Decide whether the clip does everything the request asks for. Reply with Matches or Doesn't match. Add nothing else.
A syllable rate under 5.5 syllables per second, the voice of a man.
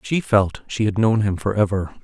Matches